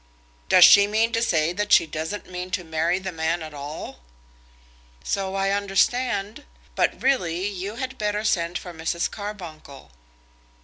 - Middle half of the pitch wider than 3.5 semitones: Yes, average, 4.0 semitones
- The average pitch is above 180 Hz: Yes, high, 190 Hz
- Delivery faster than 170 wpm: No, average, 150 wpm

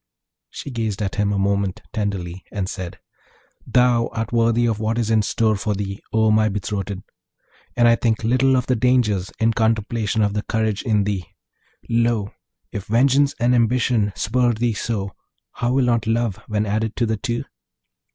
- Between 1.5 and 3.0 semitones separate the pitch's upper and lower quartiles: Yes, narrow, 2.5 semitones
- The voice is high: No, low, 110 Hz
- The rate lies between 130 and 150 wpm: No, average, 175 wpm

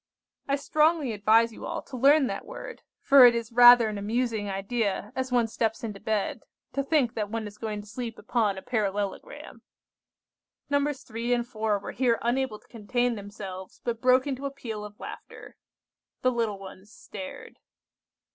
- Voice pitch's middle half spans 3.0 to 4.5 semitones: Yes, average, 3.5 semitones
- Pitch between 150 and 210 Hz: No, high, 230 Hz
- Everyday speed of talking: Yes, average, 175 wpm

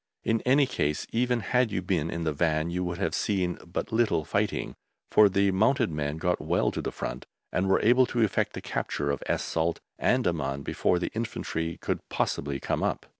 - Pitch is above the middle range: No, very low, 90 Hz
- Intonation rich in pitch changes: Yes, wide, 5.8 semitones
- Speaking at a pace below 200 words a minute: No, fast, 205 wpm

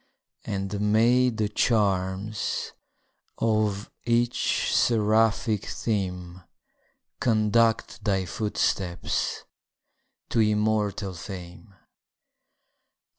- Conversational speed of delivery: No, slow, 65 wpm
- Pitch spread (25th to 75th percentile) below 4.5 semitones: Yes, narrow, 2.4 semitones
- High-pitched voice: No, low, 105 Hz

